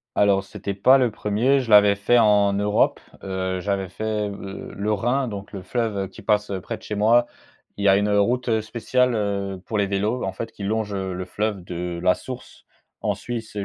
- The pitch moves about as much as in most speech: No, narrow, 2.3 semitones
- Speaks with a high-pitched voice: No, low, 105 Hz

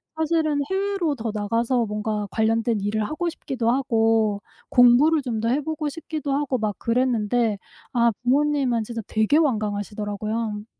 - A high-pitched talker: Yes, high, 235 Hz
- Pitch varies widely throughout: No, average, 5.0 semitones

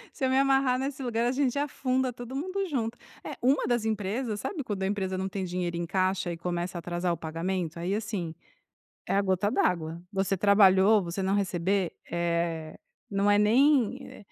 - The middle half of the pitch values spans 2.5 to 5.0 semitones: No, wide, 5.5 semitones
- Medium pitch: No, high, 200 Hz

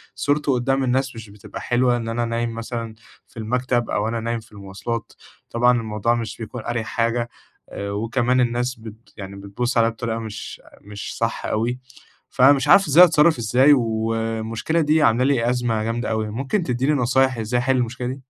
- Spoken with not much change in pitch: Yes, narrow, 2.2 semitones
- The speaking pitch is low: Yes, low, 120 Hz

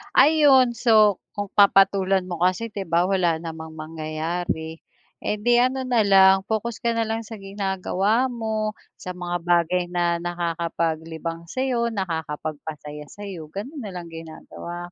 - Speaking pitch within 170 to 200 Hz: Yes, medium, 185 Hz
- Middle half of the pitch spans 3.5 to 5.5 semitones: Yes, average, 4.7 semitones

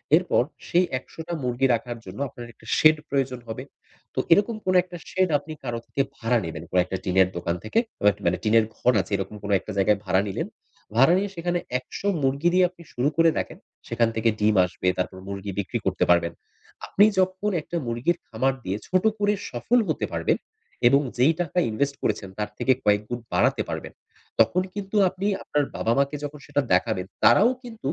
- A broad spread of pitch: Yes, wide, 8.6 semitones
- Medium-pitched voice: No, low, 125 Hz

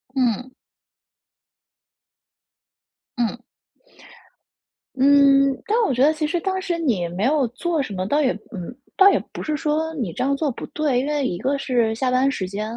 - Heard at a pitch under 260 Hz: No, very high, 270 Hz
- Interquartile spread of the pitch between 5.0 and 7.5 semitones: No, average, 4.3 semitones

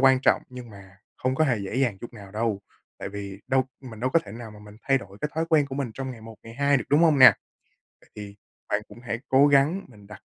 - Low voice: Yes, low, 120 Hz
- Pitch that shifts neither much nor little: Yes, average, 4.7 semitones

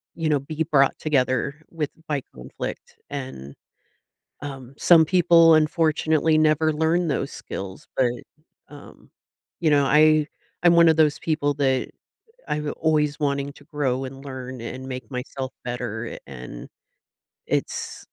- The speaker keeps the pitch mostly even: No, average, 3.1 semitones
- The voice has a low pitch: No, medium, 145 Hz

